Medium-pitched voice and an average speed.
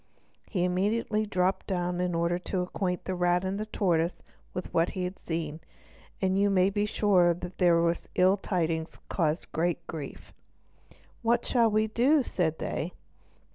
Yes: medium, 180 Hz; average, 155 wpm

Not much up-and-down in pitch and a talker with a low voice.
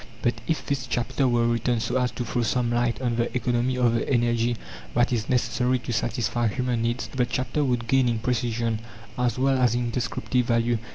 Yes: narrow, 1.3 semitones; low, 120 Hz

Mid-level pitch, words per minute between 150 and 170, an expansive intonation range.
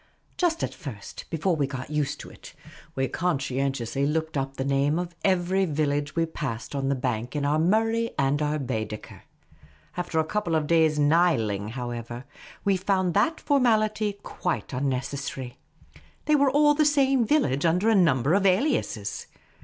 Yes: medium, 155 Hz; average, 160 wpm; wide, 6.1 semitones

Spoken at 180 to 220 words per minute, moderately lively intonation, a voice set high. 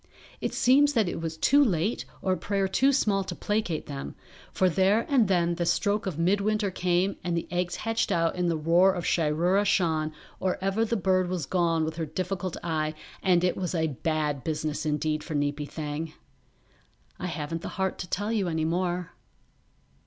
No: average, 190 wpm; average, 3.4 semitones; medium, 175 Hz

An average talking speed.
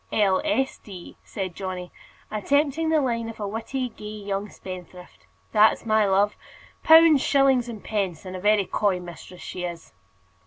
Yes: average, 160 wpm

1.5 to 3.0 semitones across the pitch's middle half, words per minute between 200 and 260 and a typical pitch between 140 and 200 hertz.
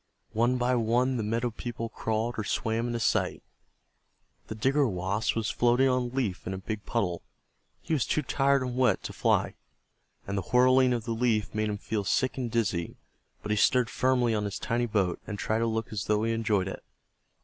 No: average, 2.7 semitones; fast, 205 wpm; low, 115 Hz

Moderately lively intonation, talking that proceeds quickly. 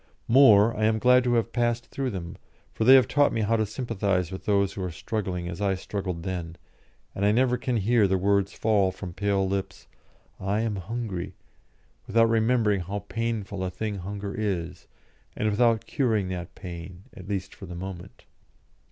No: average, 3.4 semitones; average, 185 wpm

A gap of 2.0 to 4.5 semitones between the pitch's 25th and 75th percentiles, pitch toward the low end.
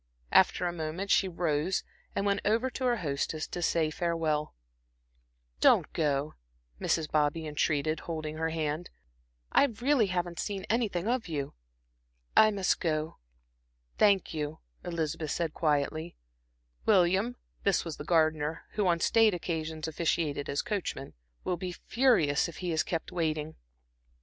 No: average, 3.7 semitones; medium, 165 Hz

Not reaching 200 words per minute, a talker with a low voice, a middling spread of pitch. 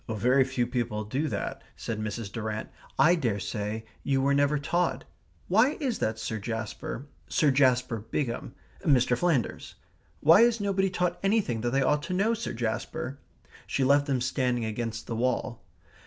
No: average, 160 wpm; low, 130 Hz; wide, 5.7 semitones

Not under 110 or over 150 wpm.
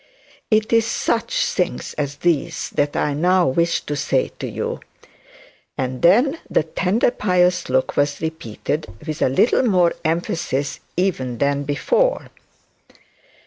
Yes: slow, 135 wpm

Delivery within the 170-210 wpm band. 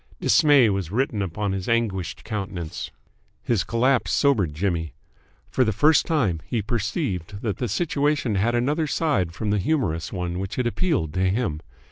No: average, 160 wpm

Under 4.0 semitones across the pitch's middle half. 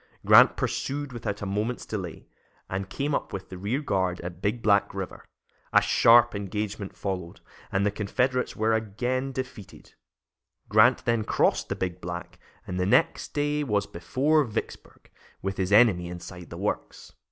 No: average, 4.6 semitones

